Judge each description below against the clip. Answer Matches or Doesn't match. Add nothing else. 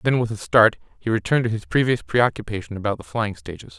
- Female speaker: Doesn't match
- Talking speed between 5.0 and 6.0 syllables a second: Doesn't match